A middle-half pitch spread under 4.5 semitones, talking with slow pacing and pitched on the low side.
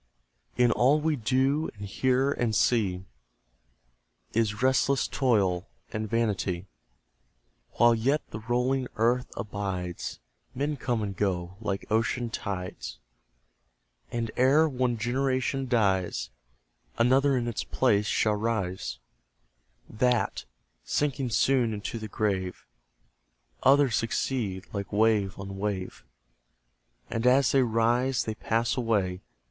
Yes: average, 4.1 semitones; slow, 115 wpm; low, 115 Hz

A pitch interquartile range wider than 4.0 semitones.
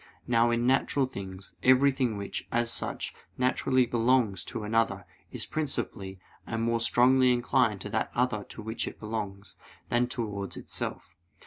No: average, 3.1 semitones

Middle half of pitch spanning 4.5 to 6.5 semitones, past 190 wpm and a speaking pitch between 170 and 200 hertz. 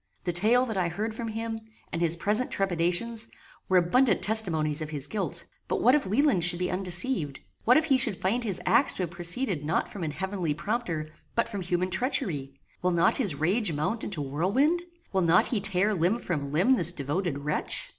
Yes: average, 5.0 semitones; average, 200 wpm; medium, 185 Hz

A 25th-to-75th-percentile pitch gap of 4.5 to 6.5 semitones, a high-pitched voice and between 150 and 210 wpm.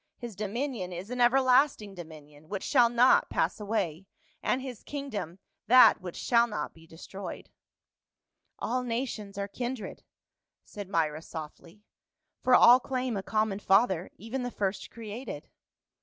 No: average, 4.8 semitones; high, 210 Hz; average, 140 wpm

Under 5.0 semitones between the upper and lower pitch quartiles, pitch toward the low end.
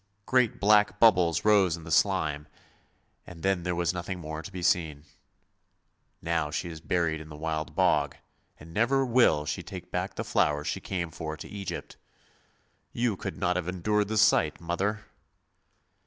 Yes: average, 4.4 semitones; very low, 90 Hz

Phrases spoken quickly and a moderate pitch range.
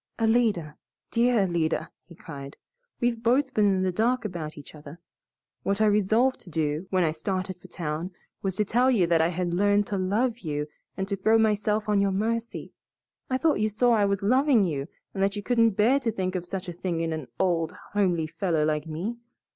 Yes: fast, 210 wpm; average, 4.7 semitones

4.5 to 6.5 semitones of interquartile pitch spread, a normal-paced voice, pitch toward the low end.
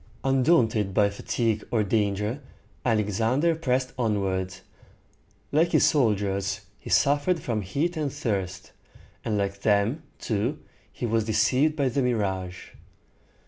No: average, 5.1 semitones; slow, 120 wpm; low, 110 Hz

